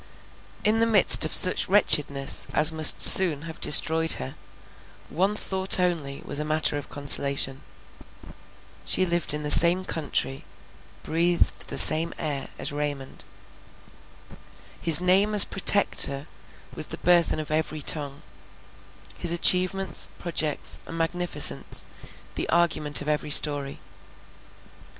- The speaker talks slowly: Yes, slow, 120 wpm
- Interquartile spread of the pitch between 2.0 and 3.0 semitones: No, average, 3.4 semitones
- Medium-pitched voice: Yes, medium, 160 Hz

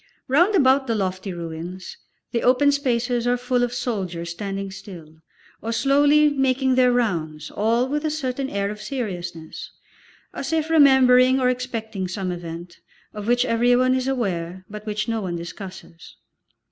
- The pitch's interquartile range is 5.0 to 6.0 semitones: Yes, wide, 5.6 semitones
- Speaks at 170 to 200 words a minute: No, average, 155 wpm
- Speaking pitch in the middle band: No, high, 230 Hz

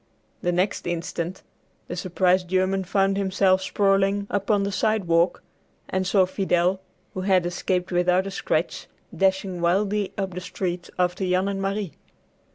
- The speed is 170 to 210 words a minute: No, average, 145 wpm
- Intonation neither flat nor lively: No, narrow, 1.6 semitones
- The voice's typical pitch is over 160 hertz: Yes, high, 190 Hz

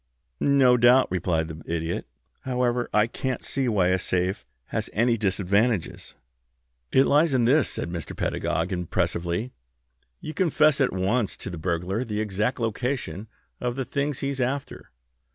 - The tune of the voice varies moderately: No, wide, 6.1 semitones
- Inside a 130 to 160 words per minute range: Yes, average, 150 wpm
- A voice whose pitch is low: Yes, low, 115 Hz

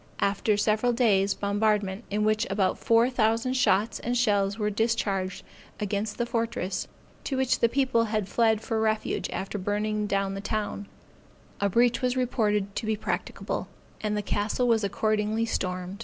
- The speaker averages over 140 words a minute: Yes, average, 160 wpm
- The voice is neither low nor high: No, high, 215 Hz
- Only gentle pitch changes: Yes, narrow, 2.2 semitones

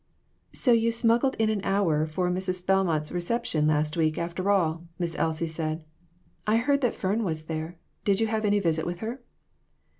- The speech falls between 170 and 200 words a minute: Yes, average, 185 wpm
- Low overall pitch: No, medium, 180 Hz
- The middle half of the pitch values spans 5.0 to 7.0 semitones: Yes, average, 5.3 semitones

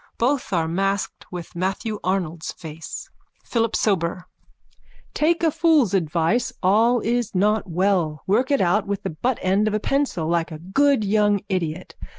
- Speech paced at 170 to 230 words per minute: No, average, 155 wpm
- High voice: Yes, high, 195 Hz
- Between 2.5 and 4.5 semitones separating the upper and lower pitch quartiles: No, average, 5.0 semitones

